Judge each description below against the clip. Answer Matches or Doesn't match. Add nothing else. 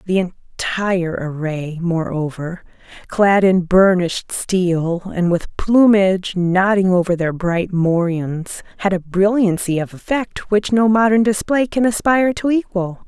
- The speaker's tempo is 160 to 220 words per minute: Doesn't match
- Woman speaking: Matches